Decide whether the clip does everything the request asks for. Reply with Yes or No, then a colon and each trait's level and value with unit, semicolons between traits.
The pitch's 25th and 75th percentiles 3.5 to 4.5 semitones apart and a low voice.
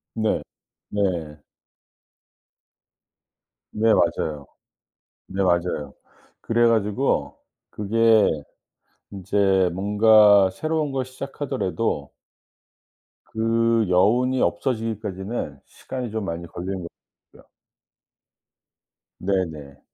Yes: average, 3.9 semitones; low, 105 Hz